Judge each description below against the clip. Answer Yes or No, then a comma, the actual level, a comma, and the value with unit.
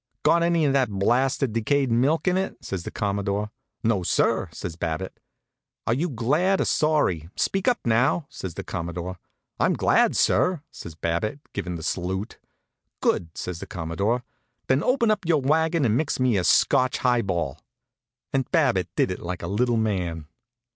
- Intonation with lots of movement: Yes, wide, 8.2 semitones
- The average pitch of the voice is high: No, low, 115 Hz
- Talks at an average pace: Yes, average, 170 wpm